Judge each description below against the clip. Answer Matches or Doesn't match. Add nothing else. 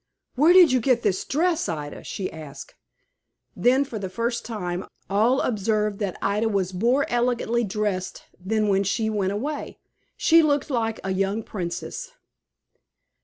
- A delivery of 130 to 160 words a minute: Matches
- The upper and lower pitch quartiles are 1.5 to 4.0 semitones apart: Doesn't match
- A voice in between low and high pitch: Doesn't match